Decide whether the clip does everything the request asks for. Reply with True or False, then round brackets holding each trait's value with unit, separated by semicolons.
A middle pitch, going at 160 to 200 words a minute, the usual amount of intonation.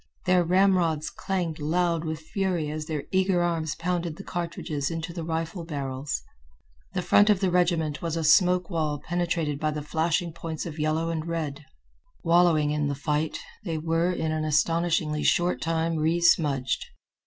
False (165 Hz; 165 wpm; 2.2 semitones)